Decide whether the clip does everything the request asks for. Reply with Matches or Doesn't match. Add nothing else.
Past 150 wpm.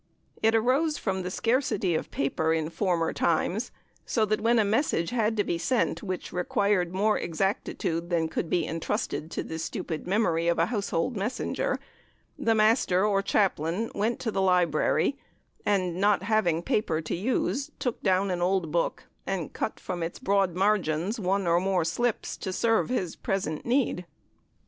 Matches